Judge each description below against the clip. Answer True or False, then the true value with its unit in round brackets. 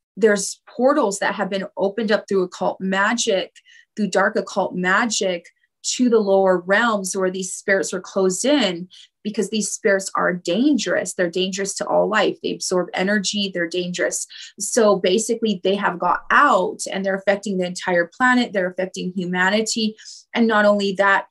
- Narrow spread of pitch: True (2.2 semitones)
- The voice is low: False (195 Hz)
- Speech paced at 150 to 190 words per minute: True (165 wpm)